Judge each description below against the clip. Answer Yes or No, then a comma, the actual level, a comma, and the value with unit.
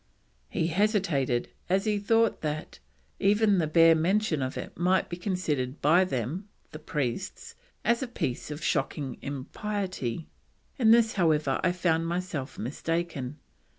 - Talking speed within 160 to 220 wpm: No, average, 140 wpm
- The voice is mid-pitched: Yes, medium, 170 Hz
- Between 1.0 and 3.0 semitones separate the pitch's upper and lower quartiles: No, average, 5.0 semitones